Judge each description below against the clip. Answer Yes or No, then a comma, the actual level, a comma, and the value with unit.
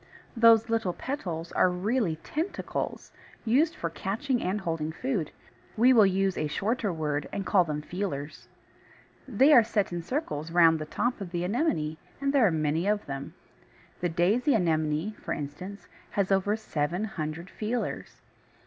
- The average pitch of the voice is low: No, high, 190 Hz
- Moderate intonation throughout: No, wide, 5.9 semitones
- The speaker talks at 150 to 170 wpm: Yes, average, 160 wpm